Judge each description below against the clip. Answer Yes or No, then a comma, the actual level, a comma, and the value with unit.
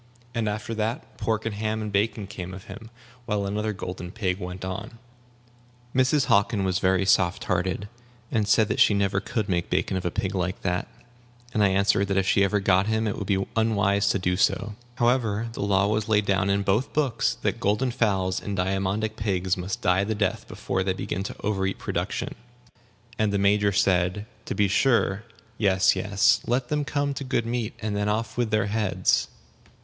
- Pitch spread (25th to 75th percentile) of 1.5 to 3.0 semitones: Yes, narrow, 2.4 semitones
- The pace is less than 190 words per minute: No, average, 195 wpm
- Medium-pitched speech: No, low, 100 Hz